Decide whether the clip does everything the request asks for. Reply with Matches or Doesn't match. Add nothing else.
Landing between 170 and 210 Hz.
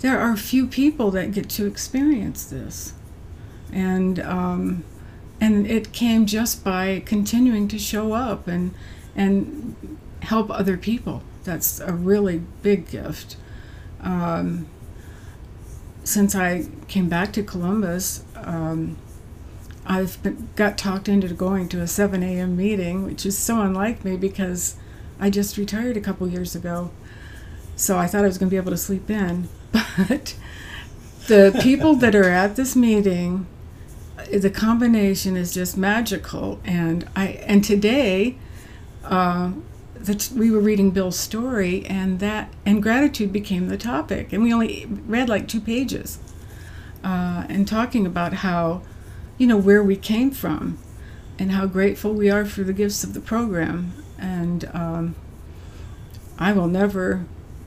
Matches